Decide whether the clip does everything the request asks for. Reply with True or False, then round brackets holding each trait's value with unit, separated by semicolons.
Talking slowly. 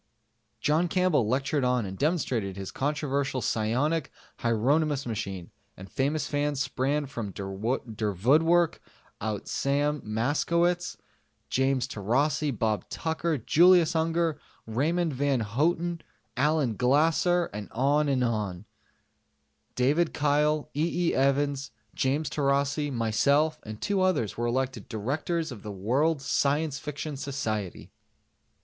True (110 wpm)